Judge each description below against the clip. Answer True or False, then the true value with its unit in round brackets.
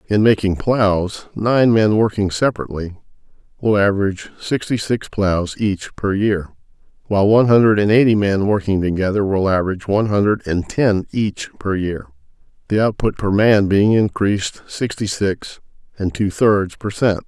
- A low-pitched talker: True (100 Hz)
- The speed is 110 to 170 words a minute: True (155 wpm)